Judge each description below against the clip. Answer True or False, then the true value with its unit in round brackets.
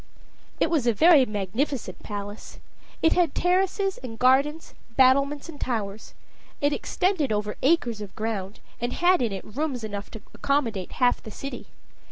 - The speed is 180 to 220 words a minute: False (155 wpm)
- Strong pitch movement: True (5.9 semitones)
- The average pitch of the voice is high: True (255 Hz)